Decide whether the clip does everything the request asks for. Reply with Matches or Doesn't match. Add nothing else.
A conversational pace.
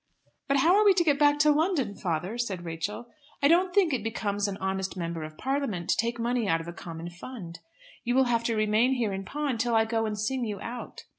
Doesn't match